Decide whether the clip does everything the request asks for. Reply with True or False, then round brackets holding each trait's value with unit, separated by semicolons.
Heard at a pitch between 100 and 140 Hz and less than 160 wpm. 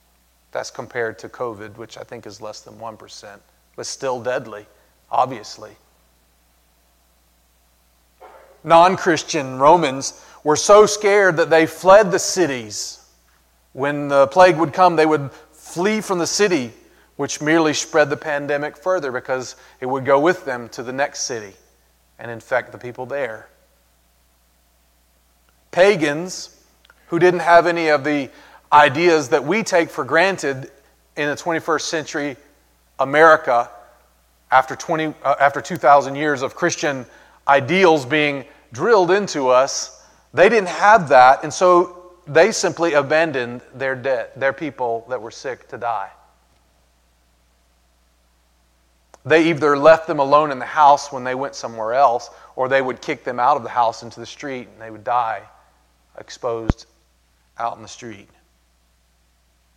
True (135 Hz; 140 wpm)